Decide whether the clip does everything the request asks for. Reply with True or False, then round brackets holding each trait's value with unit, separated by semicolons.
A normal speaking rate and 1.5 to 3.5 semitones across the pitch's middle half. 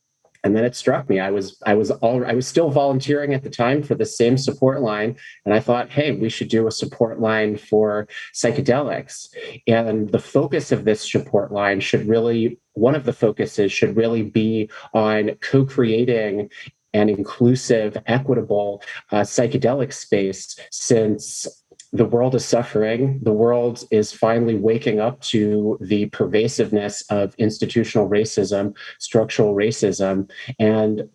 True (150 wpm; 2.4 semitones)